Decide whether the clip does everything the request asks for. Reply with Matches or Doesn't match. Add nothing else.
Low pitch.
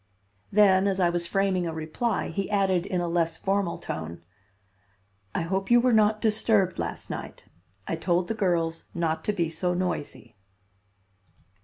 Doesn't match